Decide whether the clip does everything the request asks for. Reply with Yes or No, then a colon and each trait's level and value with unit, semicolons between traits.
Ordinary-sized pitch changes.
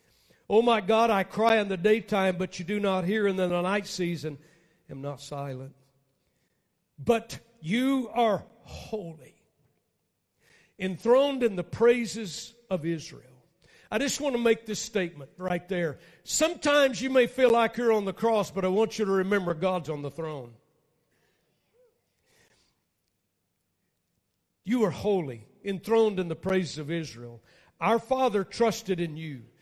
No: wide, 5.7 semitones